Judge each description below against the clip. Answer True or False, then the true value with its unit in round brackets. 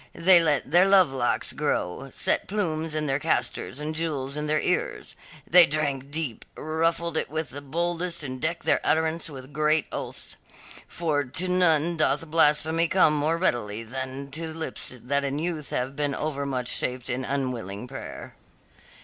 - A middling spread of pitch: True (3.4 semitones)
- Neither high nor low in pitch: True (150 Hz)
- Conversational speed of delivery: True (165 wpm)